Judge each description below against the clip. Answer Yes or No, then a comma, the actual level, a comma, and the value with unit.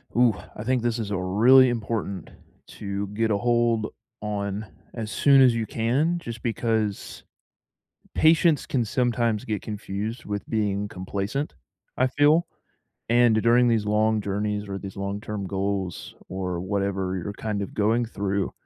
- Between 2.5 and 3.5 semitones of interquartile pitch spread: Yes, average, 2.9 semitones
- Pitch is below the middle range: Yes, low, 110 Hz